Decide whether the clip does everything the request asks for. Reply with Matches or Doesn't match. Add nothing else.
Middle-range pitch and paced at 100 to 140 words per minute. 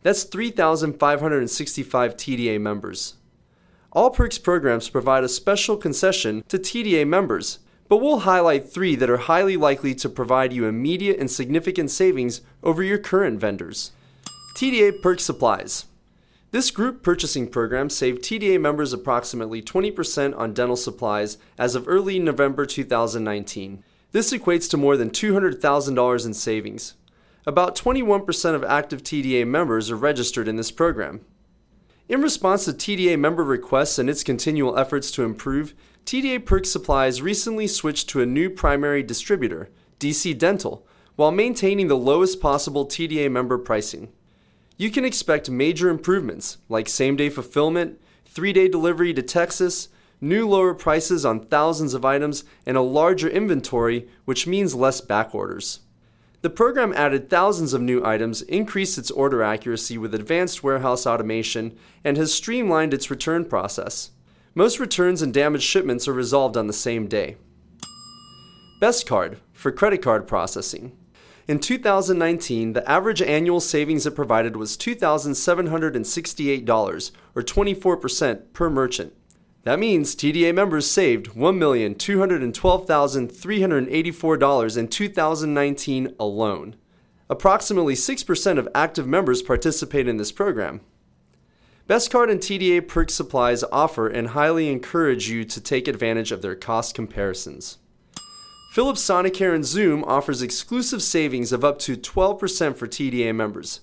Matches